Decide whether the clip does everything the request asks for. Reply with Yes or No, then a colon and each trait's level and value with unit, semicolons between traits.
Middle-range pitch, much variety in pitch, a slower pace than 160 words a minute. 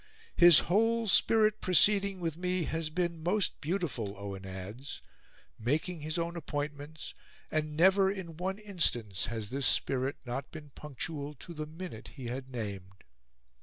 Yes: medium, 155 Hz; wide, 5.9 semitones; average, 145 wpm